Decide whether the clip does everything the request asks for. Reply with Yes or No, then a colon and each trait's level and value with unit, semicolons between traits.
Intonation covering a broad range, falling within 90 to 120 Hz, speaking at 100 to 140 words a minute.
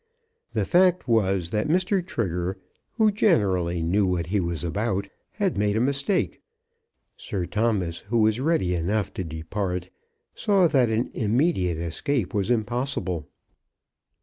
Yes: wide, 7.1 semitones; low, 105 Hz; slow, 135 wpm